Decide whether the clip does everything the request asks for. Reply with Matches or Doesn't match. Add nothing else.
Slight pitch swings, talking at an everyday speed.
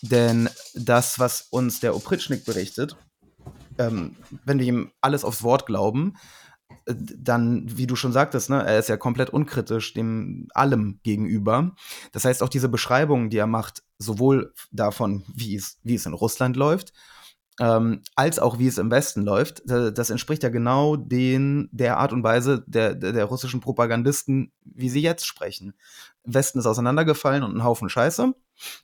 Doesn't match